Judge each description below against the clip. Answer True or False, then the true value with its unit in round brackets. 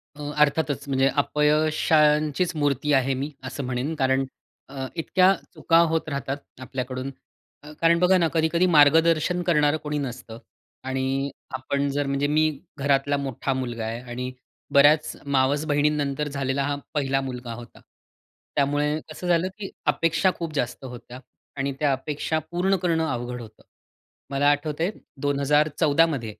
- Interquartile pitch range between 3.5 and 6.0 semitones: False (2.7 semitones)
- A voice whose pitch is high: False (145 Hz)